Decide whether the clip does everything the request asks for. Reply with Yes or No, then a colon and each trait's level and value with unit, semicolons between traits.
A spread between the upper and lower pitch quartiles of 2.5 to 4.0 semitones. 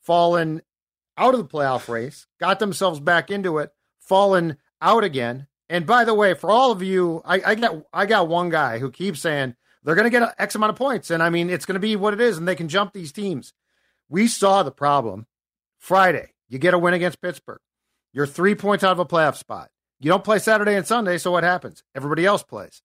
No: average, 4.5 semitones